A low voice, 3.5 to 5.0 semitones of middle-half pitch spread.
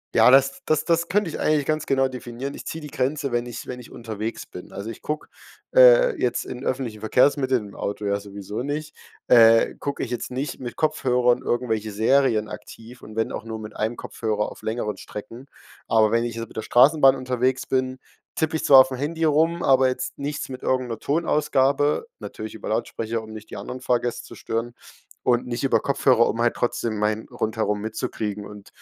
Yes: low, 125 Hz; average, 3.9 semitones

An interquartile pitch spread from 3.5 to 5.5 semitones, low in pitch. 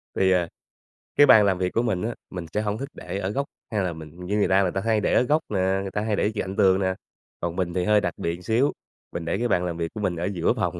No: average, 3.0 semitones; very low, 95 Hz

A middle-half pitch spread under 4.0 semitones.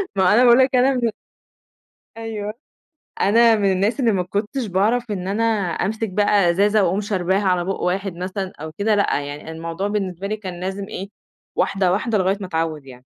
Yes: average, 2.8 semitones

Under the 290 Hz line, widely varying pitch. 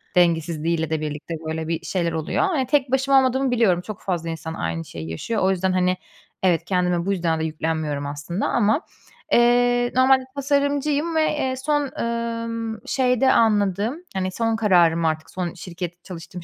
Yes: high, 190 Hz; wide, 7.0 semitones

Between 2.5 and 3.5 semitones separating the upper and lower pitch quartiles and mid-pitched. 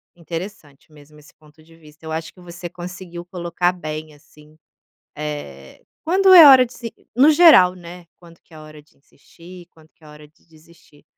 Yes: average, 2.8 semitones; medium, 165 Hz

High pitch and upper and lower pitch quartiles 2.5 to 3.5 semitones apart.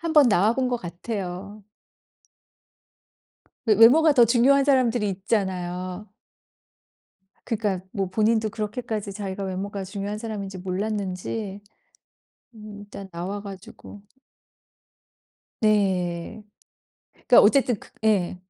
Yes: high, 205 Hz; average, 3.0 semitones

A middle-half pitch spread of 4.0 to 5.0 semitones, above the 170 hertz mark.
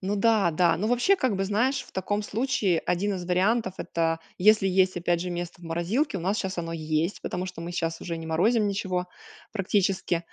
No: average, 3.3 semitones; medium, 185 Hz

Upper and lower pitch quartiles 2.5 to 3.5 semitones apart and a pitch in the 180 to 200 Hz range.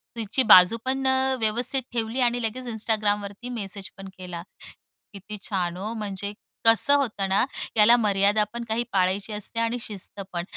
No: average, 3.2 semitones; high, 215 Hz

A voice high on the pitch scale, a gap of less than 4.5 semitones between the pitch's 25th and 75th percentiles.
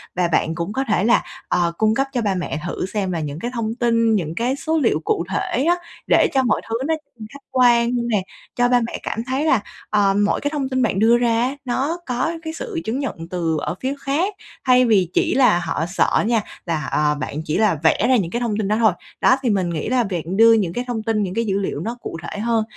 No: high, 225 Hz; average, 5.3 semitones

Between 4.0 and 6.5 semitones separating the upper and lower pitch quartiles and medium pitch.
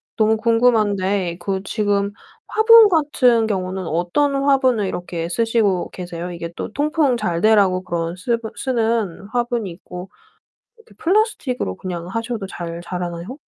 No: average, 5.3 semitones; high, 205 Hz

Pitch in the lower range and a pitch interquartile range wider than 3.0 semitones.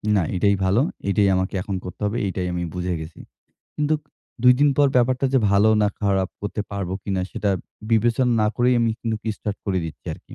Yes: low, 105 Hz; average, 4.2 semitones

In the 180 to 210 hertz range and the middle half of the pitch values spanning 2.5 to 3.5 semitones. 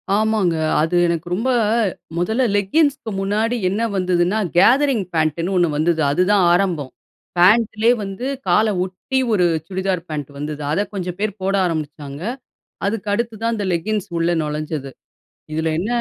No: high, 190 Hz; average, 4.6 semitones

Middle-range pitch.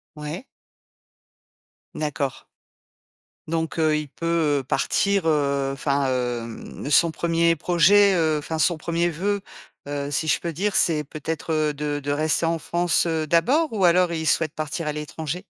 Yes: medium, 160 Hz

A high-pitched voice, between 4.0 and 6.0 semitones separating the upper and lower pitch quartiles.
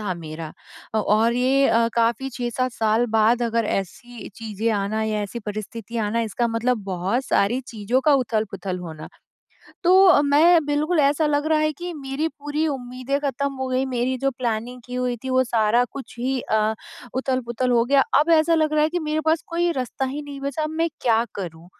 Yes: very high, 250 Hz; average, 4.5 semitones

